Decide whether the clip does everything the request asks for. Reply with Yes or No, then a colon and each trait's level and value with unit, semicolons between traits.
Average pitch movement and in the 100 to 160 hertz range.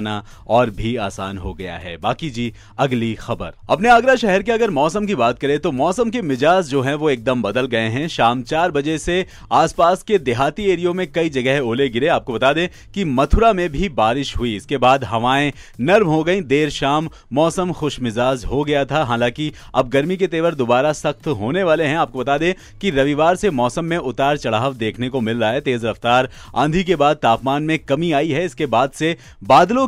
No: wide, 6.0 semitones; medium, 140 Hz